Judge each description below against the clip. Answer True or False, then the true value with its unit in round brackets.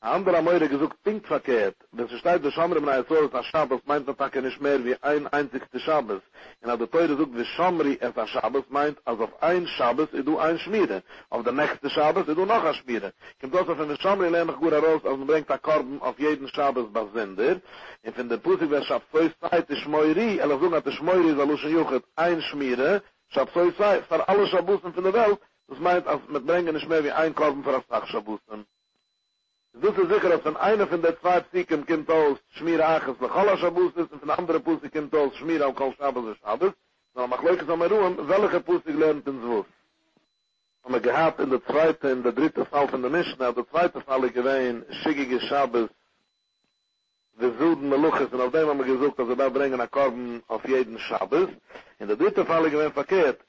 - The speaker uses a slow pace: False (195 wpm)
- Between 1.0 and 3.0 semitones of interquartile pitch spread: False (4.2 semitones)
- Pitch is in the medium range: True (155 Hz)